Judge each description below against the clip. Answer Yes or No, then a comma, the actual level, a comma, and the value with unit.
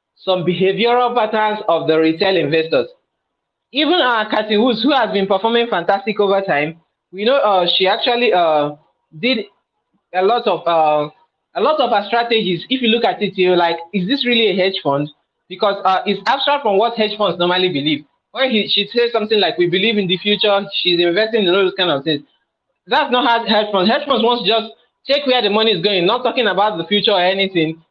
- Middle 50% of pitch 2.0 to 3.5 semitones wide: No, average, 4.3 semitones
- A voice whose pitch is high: Yes, high, 200 Hz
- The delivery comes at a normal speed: No, fast, 220 wpm